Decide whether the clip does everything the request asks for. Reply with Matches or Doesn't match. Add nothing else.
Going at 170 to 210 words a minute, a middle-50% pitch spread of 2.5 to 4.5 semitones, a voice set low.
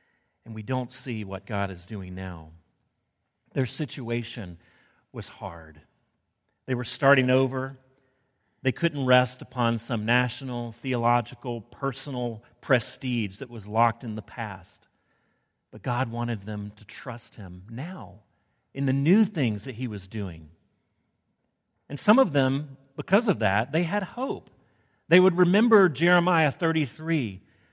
Doesn't match